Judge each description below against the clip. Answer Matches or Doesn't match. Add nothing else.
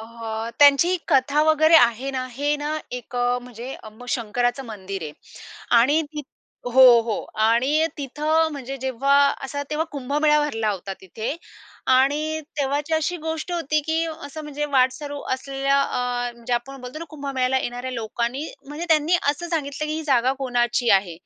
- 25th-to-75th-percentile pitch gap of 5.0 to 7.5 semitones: Doesn't match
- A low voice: Doesn't match